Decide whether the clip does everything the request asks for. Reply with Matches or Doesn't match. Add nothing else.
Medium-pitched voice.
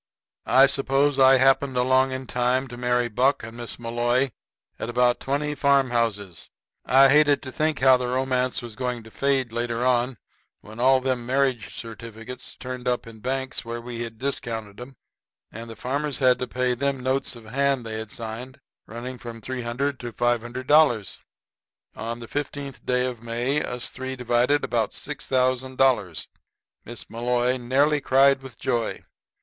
Doesn't match